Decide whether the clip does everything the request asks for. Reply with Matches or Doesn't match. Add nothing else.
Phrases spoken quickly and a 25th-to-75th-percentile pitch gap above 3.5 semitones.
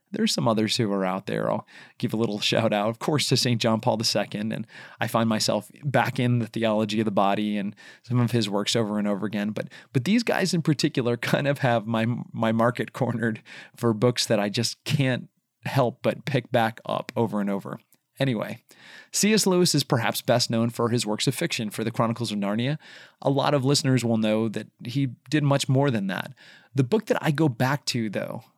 Matches